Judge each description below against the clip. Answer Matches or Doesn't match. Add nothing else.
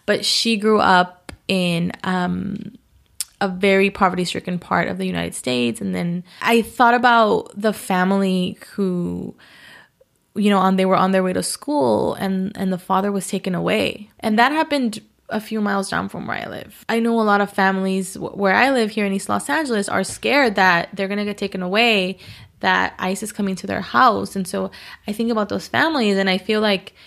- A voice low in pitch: Doesn't match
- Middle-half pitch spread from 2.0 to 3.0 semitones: Matches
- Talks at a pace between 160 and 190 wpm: Doesn't match